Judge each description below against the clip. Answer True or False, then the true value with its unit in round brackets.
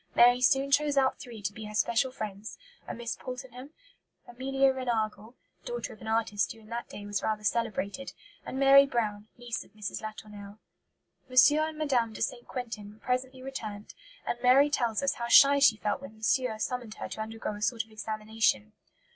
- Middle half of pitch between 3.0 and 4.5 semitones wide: True (3.3 semitones)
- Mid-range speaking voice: False (235 Hz)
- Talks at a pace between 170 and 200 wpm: True (185 wpm)